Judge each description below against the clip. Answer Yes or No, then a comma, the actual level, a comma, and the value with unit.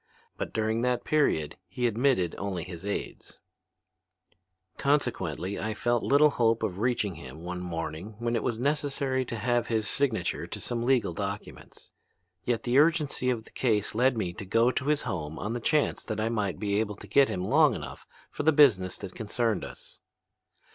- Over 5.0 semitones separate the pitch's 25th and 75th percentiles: No, average, 4.6 semitones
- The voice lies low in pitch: Yes, low, 115 Hz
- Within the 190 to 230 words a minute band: No, average, 180 wpm